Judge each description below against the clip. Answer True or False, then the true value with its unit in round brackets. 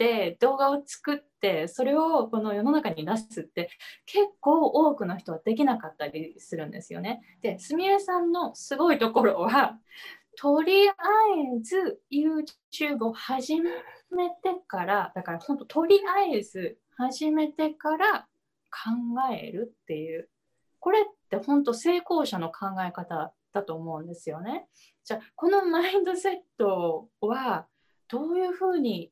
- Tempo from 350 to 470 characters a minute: False (280 characters per minute)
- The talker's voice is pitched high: True (285 Hz)